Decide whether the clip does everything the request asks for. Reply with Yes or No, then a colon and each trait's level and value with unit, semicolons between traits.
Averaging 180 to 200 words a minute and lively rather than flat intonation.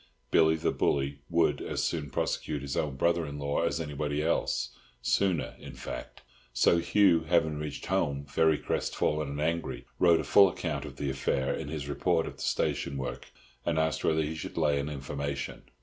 No: average, 185 wpm; average, 2.7 semitones